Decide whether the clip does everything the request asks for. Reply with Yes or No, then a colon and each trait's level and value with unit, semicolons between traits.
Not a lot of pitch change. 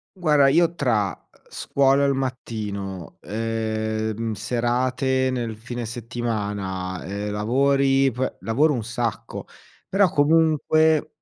No: average, 4.0 semitones